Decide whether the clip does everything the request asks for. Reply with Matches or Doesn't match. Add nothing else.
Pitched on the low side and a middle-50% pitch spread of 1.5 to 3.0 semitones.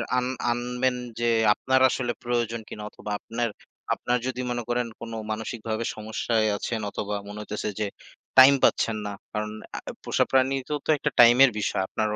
Matches